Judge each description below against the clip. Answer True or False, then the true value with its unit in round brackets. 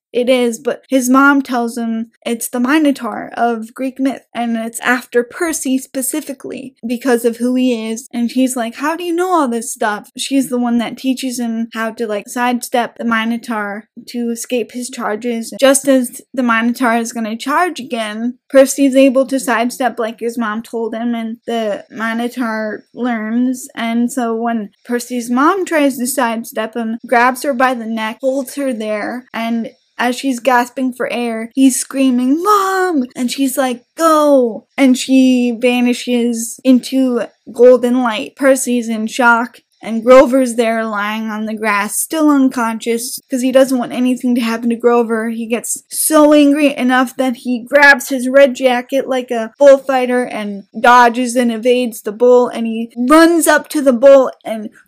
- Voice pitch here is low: False (245 Hz)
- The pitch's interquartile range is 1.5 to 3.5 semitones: True (2.4 semitones)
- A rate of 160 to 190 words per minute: True (170 wpm)